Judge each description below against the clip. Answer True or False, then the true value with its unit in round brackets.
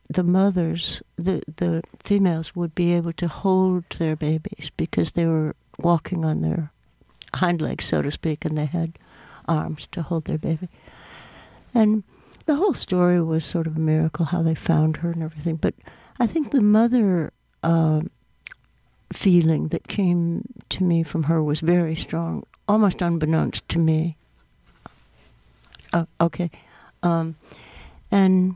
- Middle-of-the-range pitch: True (170 Hz)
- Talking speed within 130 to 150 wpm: True (145 wpm)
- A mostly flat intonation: True (2.3 semitones)